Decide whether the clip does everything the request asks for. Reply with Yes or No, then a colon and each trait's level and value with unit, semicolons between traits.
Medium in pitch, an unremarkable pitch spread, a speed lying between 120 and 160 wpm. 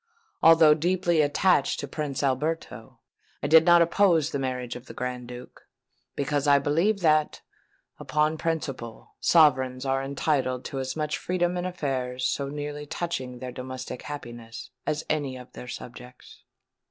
Yes: medium, 145 Hz; average, 3.8 semitones; average, 150 wpm